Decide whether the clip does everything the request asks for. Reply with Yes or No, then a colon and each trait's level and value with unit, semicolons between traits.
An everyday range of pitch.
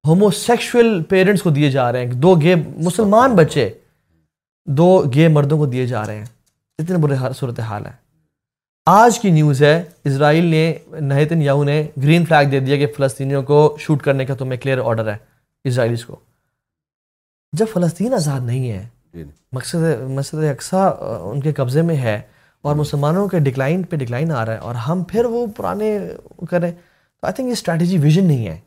Yes: average, 4.5 semitones